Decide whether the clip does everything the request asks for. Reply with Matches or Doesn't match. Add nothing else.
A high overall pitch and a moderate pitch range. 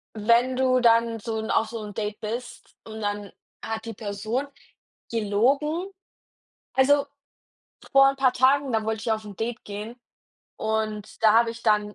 Matches